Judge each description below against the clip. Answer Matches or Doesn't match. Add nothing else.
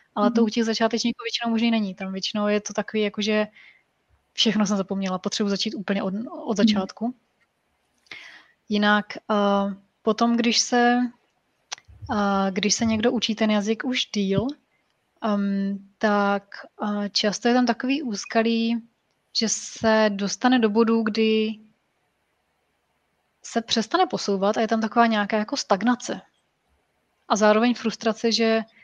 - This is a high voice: Matches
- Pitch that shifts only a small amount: Matches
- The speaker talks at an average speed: Matches